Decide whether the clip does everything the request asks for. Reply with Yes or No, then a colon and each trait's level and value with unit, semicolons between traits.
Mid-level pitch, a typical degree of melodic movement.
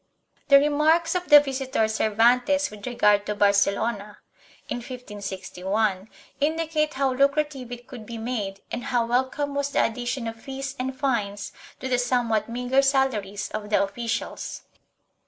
No: high, 245 Hz; average, 4.5 semitones